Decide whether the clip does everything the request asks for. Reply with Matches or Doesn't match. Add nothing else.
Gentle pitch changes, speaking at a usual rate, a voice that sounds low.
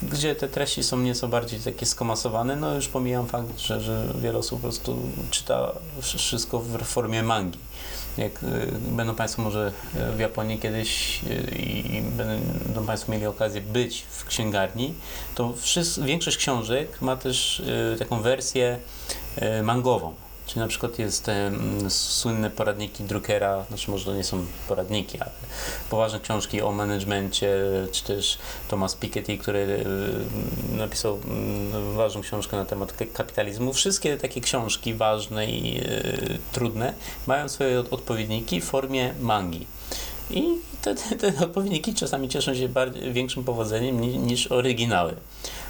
Doesn't match